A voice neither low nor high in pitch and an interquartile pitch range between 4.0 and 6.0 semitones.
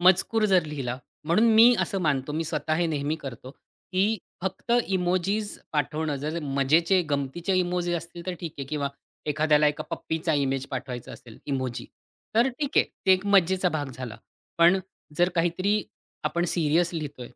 Yes: medium, 165 Hz; average, 4.3 semitones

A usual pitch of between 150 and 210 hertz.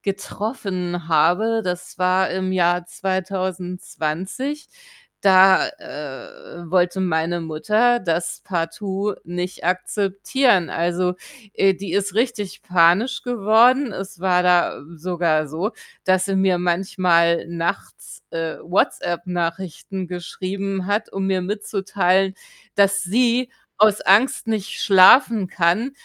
Yes: medium, 185 Hz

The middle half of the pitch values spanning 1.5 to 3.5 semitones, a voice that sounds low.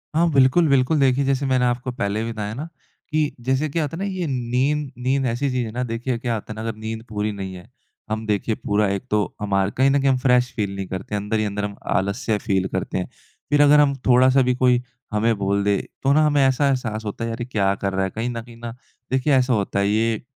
No: average, 4.2 semitones; low, 120 Hz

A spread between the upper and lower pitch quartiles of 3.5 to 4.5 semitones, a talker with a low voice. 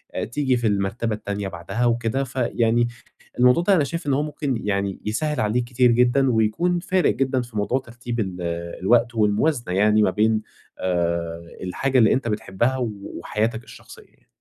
Yes: average, 3.9 semitones; low, 120 Hz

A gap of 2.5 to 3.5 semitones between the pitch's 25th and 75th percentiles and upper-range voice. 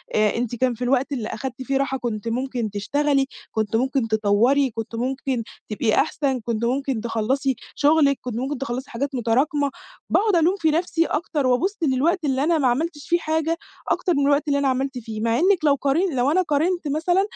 No: average, 3.9 semitones; very high, 270 Hz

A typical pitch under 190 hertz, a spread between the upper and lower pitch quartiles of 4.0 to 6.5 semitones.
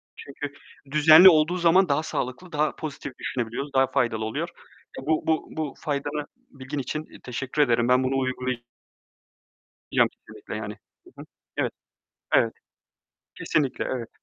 No: medium, 140 Hz; average, 3.2 semitones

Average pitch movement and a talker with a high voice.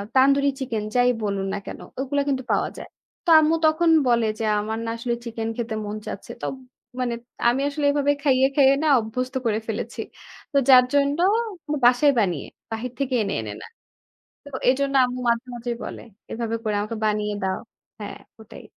Yes: average, 3.9 semitones; high, 245 Hz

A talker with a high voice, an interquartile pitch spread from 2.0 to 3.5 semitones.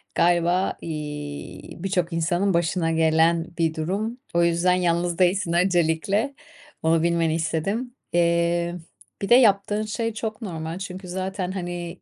No: medium, 175 Hz; narrow, 2.6 semitones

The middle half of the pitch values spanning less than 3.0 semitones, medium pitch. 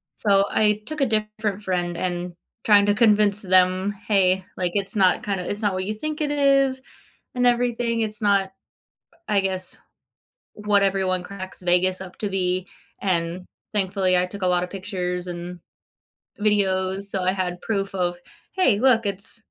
No: narrow, 2.5 semitones; high, 195 Hz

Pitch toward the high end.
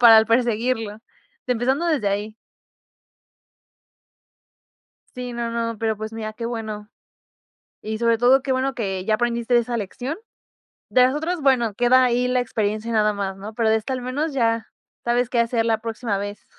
Yes: high, 230 Hz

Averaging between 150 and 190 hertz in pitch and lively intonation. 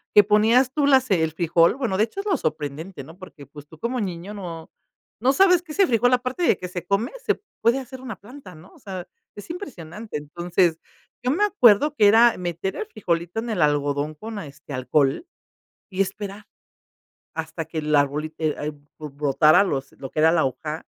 Yes: medium, 185 Hz; wide, 7.1 semitones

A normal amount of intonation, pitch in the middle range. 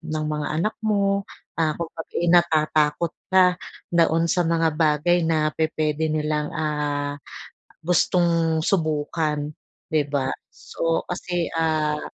No: narrow, 2.1 semitones; medium, 160 Hz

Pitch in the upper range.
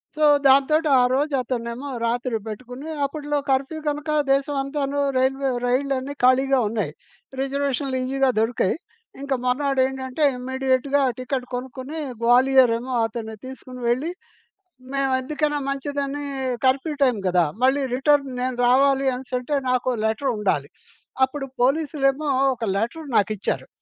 Yes: very high, 265 Hz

